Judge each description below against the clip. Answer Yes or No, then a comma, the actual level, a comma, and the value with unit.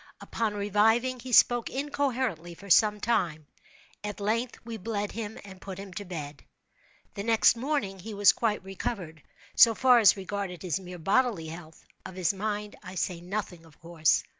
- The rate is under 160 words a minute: No, average, 170 wpm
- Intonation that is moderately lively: Yes, average, 4.1 semitones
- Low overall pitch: No, high, 200 Hz